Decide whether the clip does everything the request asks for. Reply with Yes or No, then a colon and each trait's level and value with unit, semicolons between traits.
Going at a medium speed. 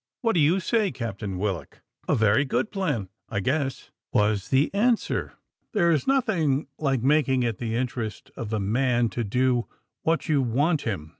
Yes: average, 170 wpm